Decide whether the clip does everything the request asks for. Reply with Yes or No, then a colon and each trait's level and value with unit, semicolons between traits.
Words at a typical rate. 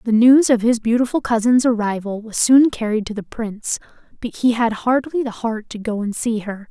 No: fast, 215 wpm